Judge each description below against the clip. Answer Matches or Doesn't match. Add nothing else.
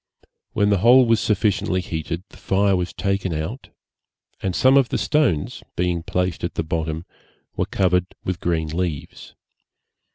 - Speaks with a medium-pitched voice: Doesn't match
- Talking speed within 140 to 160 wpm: Matches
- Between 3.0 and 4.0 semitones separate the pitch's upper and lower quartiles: Matches